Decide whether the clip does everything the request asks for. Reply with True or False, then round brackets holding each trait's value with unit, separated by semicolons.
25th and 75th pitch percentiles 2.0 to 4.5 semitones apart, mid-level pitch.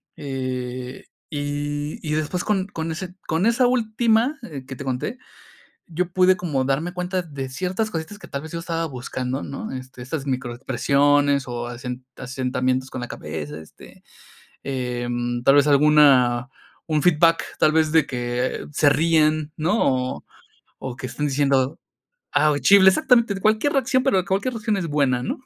False (5.5 semitones; 145 Hz)